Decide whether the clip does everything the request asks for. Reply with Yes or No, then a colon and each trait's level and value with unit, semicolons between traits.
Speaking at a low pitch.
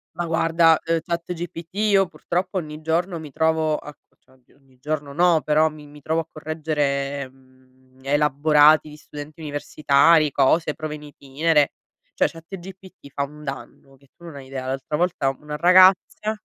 No: medium, 150 Hz